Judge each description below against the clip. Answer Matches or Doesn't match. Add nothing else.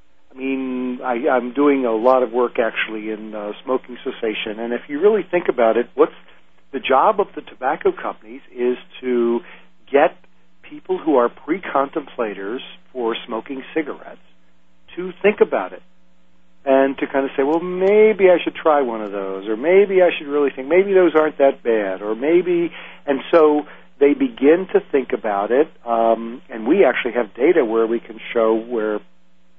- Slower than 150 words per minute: Doesn't match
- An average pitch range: Doesn't match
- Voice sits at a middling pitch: Doesn't match